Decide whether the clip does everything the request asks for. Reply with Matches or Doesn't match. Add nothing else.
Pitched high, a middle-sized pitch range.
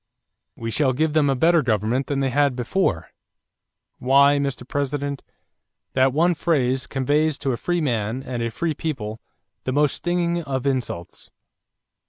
Doesn't match